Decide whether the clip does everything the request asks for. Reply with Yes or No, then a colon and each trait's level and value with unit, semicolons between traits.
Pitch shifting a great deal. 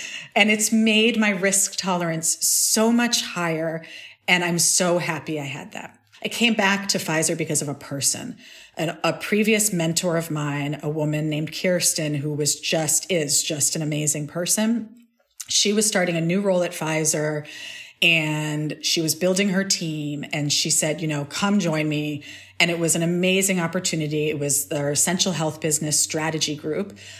No: average, 3.8 semitones